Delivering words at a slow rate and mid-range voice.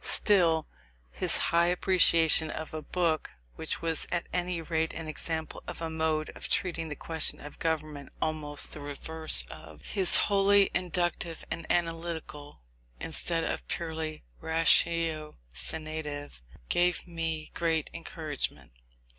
Yes: slow, 125 wpm; medium, 160 Hz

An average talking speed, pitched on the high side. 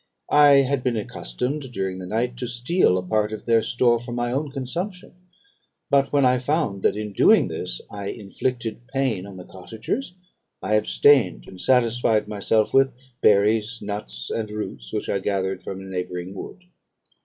No: average, 170 wpm; low, 110 Hz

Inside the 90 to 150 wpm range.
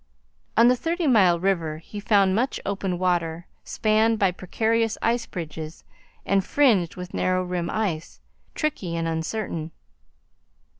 Yes: slow, 135 wpm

